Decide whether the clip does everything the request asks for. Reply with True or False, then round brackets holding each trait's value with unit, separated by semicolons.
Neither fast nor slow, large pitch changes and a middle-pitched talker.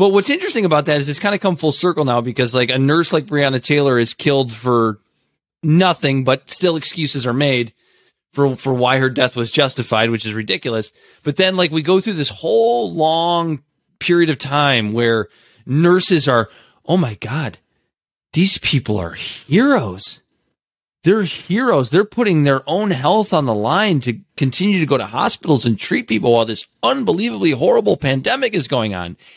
True (180 wpm; 6.3 semitones; 145 Hz)